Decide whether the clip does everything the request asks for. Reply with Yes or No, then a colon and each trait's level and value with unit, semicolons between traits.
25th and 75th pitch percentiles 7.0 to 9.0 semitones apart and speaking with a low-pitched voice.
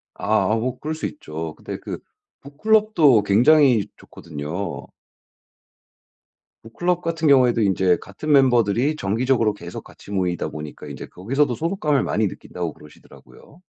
Yes: wide, 7.6 semitones; low, 120 Hz